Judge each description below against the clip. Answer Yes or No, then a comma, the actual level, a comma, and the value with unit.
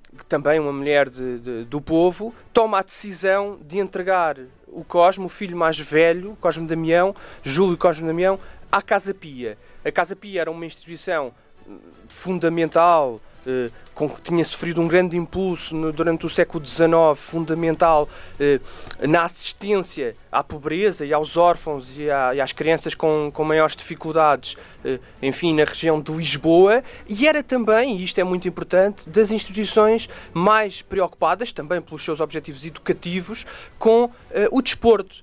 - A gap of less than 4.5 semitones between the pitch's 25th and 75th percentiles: Yes, average, 3.6 semitones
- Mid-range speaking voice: Yes, medium, 165 Hz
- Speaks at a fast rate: No, average, 155 wpm